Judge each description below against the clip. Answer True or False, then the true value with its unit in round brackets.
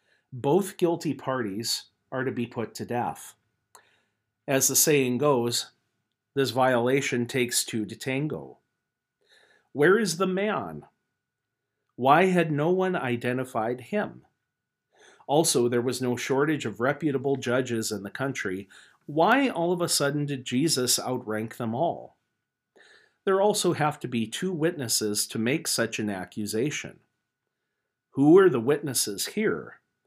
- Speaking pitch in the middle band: False (130 Hz)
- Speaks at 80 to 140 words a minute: True (135 wpm)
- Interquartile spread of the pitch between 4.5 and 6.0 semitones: True (5.6 semitones)